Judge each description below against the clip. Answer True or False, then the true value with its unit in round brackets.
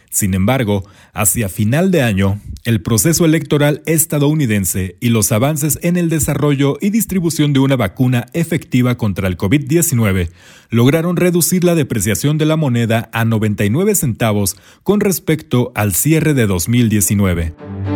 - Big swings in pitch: True (7.1 semitones)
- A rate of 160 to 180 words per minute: False (135 wpm)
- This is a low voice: True (125 Hz)